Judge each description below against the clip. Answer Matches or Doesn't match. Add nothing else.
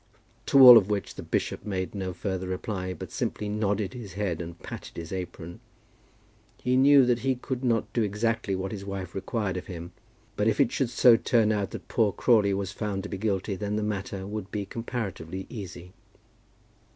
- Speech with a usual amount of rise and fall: Matches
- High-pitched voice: Doesn't match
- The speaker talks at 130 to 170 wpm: Doesn't match